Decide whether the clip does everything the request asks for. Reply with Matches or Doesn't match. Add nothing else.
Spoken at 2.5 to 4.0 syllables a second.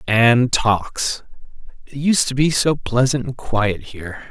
Matches